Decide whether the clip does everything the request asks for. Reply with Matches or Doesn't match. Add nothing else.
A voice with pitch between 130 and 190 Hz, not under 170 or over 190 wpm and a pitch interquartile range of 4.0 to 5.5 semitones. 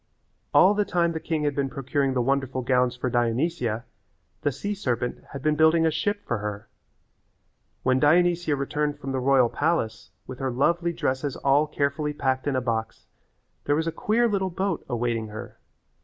Matches